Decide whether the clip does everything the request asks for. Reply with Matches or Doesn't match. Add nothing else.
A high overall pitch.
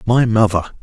Doesn't match